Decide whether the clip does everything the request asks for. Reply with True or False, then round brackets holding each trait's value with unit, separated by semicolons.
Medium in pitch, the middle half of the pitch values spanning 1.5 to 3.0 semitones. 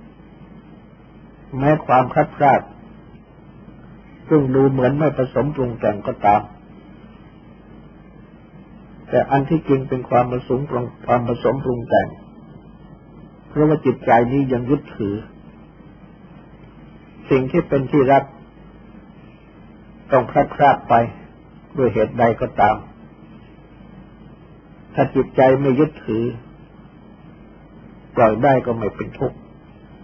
False (130 Hz; 2.6 semitones)